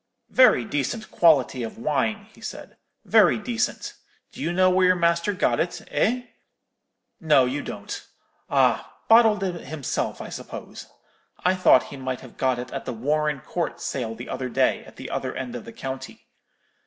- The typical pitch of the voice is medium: Yes, medium, 150 Hz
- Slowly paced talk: No, average, 175 wpm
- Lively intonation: Yes, wide, 6.2 semitones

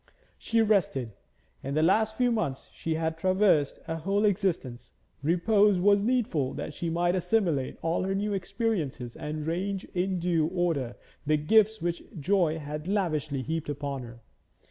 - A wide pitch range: No, average, 5.0 semitones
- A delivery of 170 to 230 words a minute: No, average, 155 wpm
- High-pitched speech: No, medium, 170 Hz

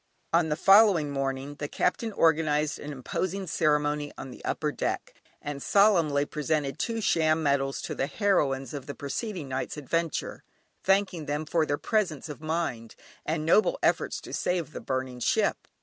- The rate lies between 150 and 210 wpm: Yes, average, 165 wpm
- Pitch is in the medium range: Yes, medium, 150 Hz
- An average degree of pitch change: Yes, average, 3.3 semitones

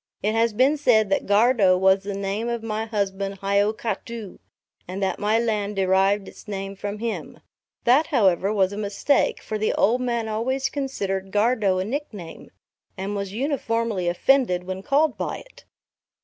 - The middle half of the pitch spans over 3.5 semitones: No, average, 3.2 semitones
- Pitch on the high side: Yes, high, 210 Hz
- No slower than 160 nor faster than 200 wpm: Yes, average, 165 wpm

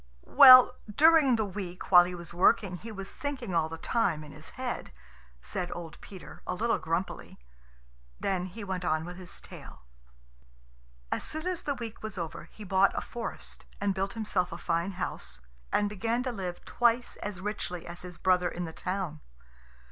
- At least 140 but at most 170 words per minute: No, average, 180 wpm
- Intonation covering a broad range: No, average, 4.5 semitones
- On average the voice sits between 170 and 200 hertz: Yes, high, 190 Hz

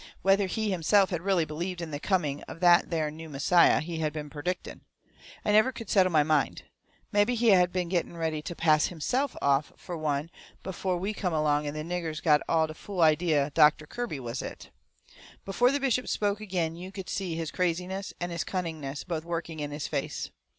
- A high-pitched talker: No, medium, 170 Hz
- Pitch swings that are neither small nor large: Yes, average, 3.6 semitones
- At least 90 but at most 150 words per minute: No, fast, 205 wpm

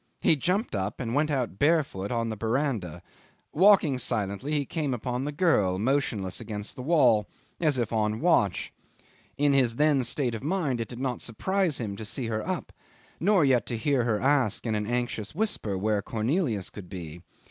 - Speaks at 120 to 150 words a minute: No, average, 190 wpm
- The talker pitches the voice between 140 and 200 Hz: No, low, 125 Hz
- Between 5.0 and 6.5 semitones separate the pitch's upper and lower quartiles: Yes, wide, 5.4 semitones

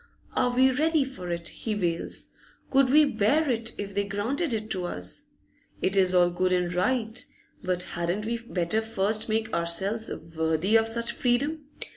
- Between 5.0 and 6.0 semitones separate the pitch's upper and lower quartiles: Yes, average, 5.3 semitones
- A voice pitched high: Yes, high, 215 Hz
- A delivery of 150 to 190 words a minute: Yes, average, 170 wpm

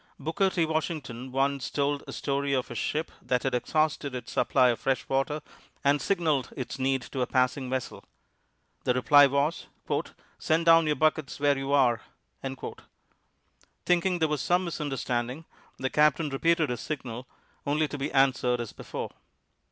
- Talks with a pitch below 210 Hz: Yes, medium, 140 Hz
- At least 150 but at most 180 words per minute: Yes, average, 160 wpm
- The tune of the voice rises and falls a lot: No, average, 3.2 semitones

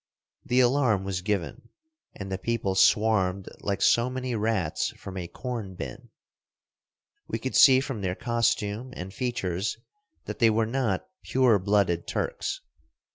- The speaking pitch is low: Yes, low, 110 Hz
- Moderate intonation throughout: Yes, average, 4.3 semitones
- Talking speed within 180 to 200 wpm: No, average, 140 wpm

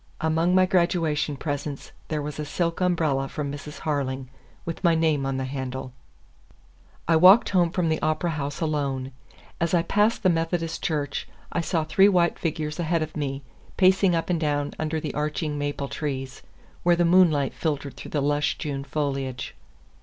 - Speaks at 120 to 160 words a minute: No, average, 175 wpm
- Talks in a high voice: No, medium, 155 Hz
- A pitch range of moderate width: Yes, average, 3.0 semitones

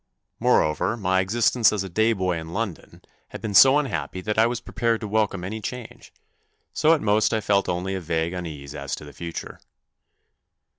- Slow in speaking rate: No, average, 190 wpm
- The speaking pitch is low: Yes, low, 100 Hz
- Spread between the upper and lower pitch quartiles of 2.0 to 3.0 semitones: No, average, 4.4 semitones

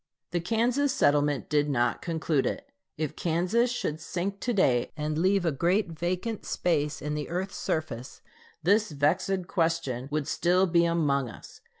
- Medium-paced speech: Yes, average, 160 wpm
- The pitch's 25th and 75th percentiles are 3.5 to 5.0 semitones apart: Yes, average, 4.2 semitones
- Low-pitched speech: No, medium, 170 Hz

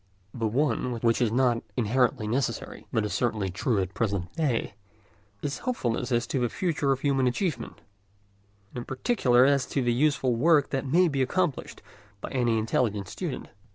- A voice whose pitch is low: Yes, low, 125 Hz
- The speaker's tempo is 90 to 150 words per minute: No, average, 175 wpm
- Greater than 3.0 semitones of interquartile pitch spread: Yes, average, 3.4 semitones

